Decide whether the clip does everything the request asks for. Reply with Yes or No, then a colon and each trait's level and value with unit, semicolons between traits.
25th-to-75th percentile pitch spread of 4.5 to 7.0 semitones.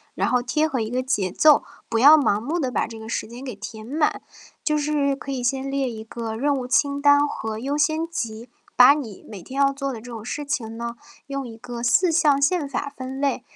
No: average, 3.7 semitones